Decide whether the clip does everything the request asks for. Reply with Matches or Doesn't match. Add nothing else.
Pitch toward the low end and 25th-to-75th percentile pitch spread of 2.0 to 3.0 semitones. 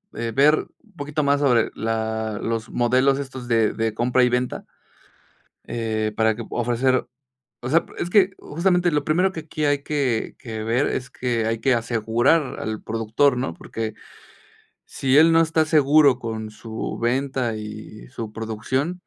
Doesn't match